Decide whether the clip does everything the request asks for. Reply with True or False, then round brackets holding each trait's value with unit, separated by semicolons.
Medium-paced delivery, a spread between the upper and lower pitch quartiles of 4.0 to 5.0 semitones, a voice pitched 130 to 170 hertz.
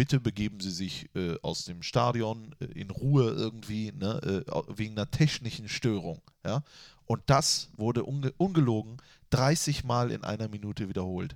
False (160 wpm; 4.4 semitones; 115 Hz)